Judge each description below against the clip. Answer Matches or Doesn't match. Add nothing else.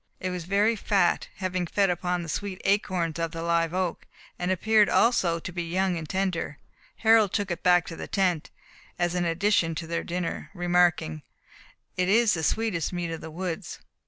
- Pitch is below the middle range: Doesn't match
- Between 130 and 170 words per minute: Doesn't match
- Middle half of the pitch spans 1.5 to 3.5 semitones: Matches